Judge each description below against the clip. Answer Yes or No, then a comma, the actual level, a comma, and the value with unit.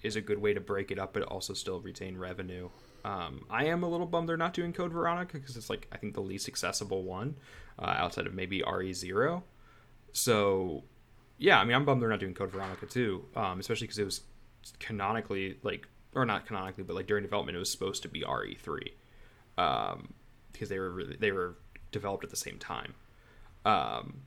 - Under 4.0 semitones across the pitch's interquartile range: No, average, 4.6 semitones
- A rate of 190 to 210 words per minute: Yes, fast, 205 wpm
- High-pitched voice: No, low, 105 Hz